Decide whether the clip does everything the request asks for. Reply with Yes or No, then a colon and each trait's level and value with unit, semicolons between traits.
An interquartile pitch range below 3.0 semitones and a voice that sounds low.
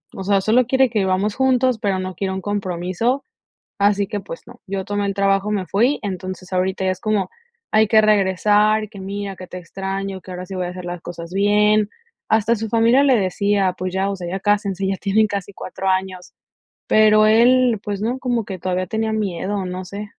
No: narrow, 2.4 semitones; high, 200 Hz